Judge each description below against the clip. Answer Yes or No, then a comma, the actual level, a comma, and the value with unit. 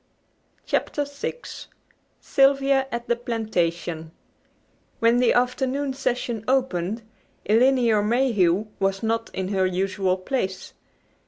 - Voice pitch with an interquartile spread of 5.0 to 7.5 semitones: Yes, average, 5.3 semitones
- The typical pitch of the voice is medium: No, high, 230 Hz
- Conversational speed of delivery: No, slow, 100 wpm